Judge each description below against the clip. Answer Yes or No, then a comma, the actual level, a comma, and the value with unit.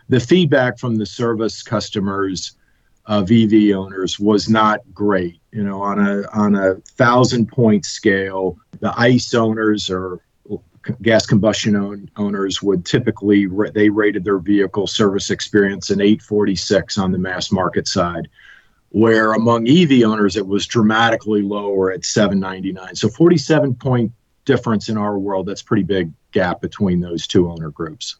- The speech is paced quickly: No, average, 145 wpm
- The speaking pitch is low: Yes, low, 105 Hz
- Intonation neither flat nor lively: No, narrow, 2.3 semitones